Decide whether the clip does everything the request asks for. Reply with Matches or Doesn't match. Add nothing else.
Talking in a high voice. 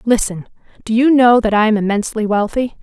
Matches